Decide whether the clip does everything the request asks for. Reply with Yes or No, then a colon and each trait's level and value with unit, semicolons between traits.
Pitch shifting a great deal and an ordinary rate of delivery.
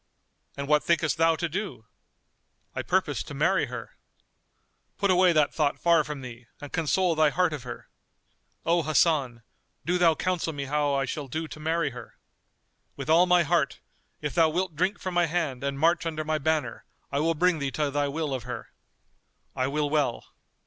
No: average, 3.1 semitones; average, 190 wpm